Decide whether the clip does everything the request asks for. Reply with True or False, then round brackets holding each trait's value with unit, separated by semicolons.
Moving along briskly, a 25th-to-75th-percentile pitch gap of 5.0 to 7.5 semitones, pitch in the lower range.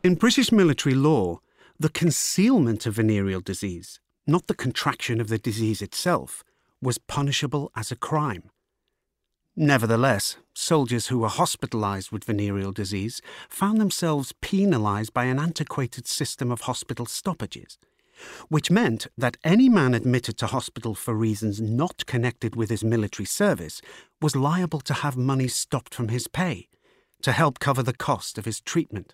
False (150 wpm; 5.4 semitones; 125 Hz)